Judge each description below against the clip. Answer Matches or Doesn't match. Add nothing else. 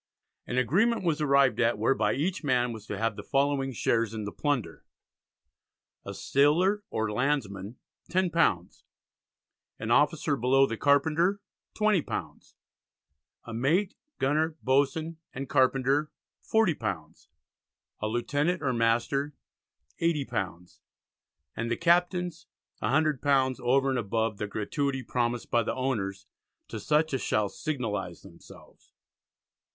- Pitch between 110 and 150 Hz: Matches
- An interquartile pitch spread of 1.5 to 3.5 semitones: Doesn't match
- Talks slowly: Matches